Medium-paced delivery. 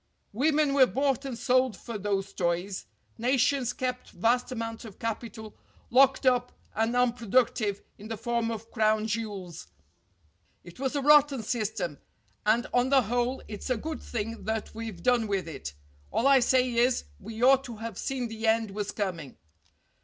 Yes: average, 165 wpm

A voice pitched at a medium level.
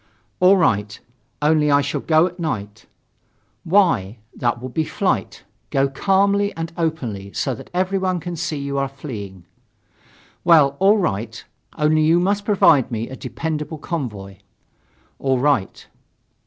Yes: medium, 150 Hz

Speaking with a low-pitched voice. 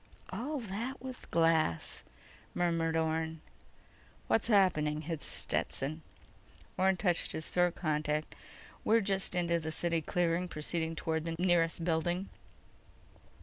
No: medium, 170 Hz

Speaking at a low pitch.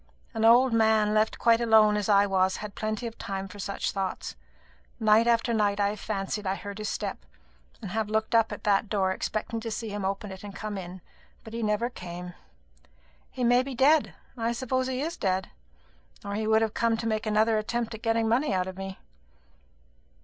No: high, 215 Hz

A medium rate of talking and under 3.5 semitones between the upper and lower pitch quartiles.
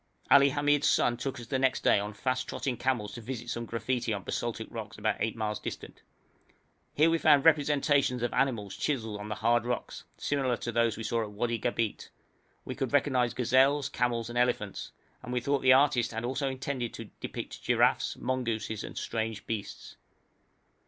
Yes: average, 185 wpm; average, 2.9 semitones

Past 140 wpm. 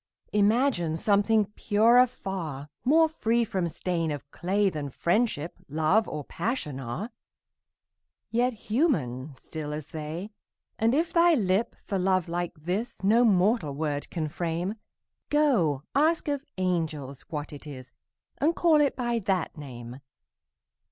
No: slow, 135 wpm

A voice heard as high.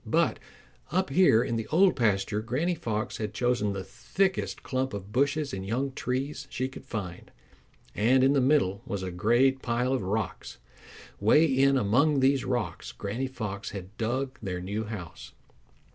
No: low, 120 Hz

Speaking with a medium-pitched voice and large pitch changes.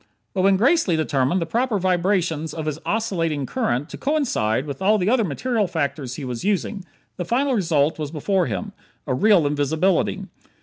Yes: medium, 175 Hz; wide, 6.0 semitones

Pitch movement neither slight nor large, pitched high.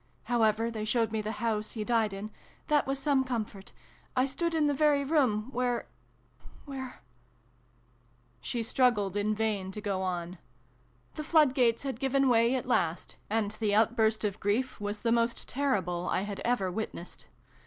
Yes: average, 3.9 semitones; high, 225 Hz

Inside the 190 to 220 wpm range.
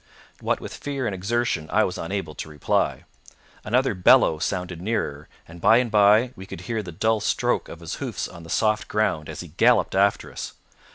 Yes: average, 195 wpm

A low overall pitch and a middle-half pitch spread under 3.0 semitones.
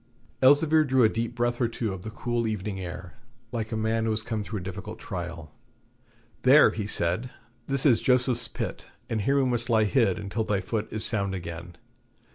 No: low, 110 Hz; average, 3.8 semitones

